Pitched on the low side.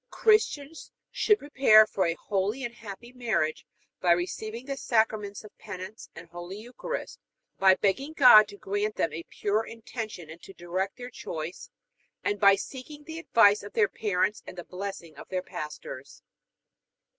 No: high, 205 Hz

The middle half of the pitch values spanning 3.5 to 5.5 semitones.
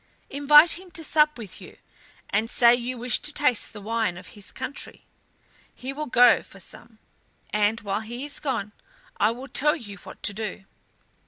Yes: average, 5.2 semitones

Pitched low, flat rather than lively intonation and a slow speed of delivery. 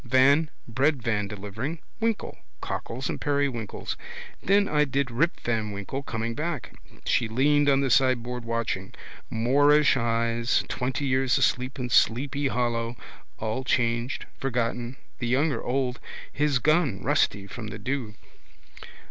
No: low, 125 Hz; average, 3.4 semitones; slow, 130 wpm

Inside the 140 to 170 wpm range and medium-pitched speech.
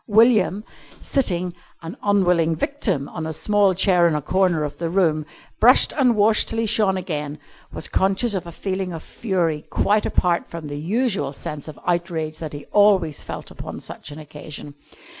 No: average, 180 wpm; medium, 175 Hz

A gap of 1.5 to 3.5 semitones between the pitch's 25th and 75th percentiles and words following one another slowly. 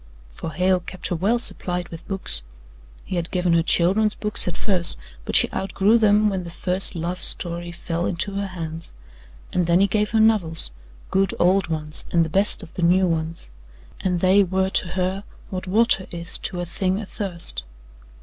No: narrow, 2.4 semitones; average, 190 wpm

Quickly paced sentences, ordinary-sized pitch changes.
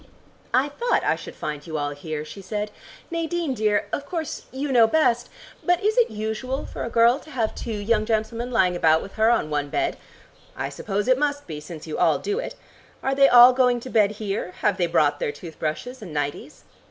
No: fast, 215 wpm; wide, 7.1 semitones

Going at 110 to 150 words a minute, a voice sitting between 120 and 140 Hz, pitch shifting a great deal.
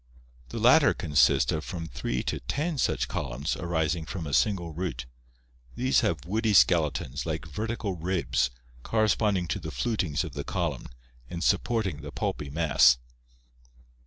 No: average, 145 wpm; very low, 85 Hz; wide, 6.2 semitones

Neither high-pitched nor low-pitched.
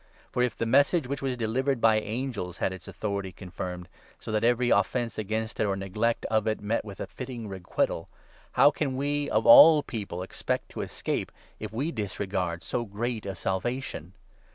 No: low, 110 Hz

